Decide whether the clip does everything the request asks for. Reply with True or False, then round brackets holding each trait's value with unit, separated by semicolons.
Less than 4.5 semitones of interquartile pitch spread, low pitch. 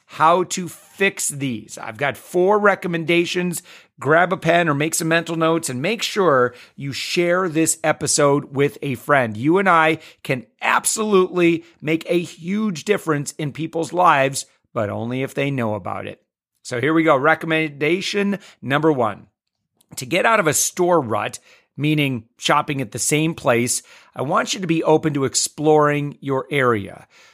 False (3.9 semitones; 155 Hz)